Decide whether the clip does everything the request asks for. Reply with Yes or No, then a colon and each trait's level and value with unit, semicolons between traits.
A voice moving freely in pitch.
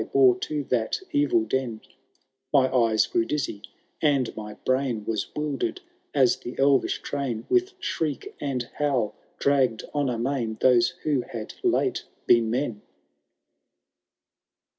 No: average, 3.6 semitones